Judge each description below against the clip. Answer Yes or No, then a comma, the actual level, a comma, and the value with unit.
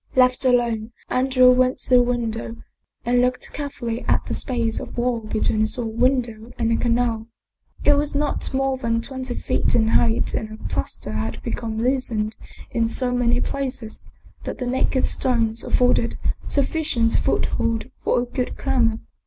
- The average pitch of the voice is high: Yes, high, 245 Hz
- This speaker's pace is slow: No, average, 165 wpm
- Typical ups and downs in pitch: No, narrow, 2.0 semitones